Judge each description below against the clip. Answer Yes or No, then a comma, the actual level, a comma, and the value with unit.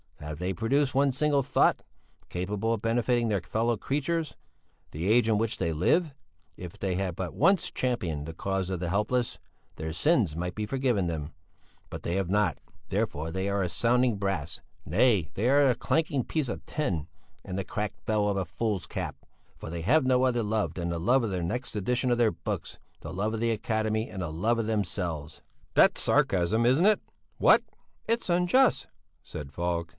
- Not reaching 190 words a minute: No, average, 195 wpm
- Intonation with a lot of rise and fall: Yes, wide, 5.8 semitones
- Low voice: Yes, low, 105 Hz